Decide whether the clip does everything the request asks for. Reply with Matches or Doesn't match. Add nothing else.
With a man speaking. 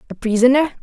Doesn't match